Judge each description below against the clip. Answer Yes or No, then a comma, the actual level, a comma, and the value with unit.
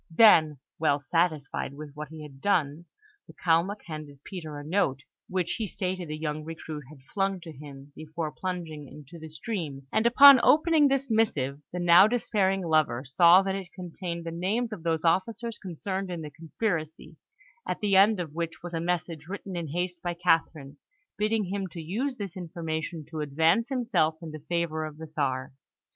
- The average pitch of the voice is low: No, medium, 170 Hz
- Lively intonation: No, average, 3.9 semitones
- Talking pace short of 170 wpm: No, average, 185 wpm